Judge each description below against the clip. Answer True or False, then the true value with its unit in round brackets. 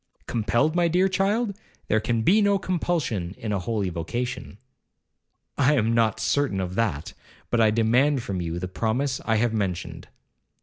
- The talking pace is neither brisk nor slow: True (165 wpm)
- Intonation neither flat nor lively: False (6.6 semitones)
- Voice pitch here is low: True (115 Hz)